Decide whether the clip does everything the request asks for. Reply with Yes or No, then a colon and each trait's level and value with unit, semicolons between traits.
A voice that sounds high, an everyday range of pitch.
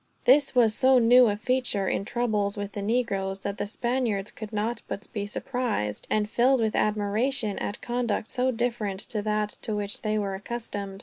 Yes: high, 215 Hz; average, 3.1 semitones